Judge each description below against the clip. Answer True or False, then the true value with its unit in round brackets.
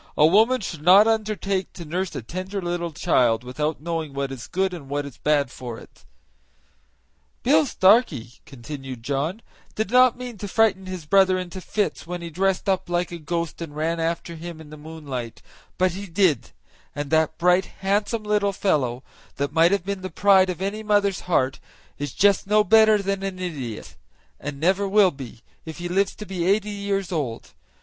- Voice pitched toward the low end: False (180 Hz)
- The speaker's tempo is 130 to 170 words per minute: False (190 wpm)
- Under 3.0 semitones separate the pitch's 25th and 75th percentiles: False (4.8 semitones)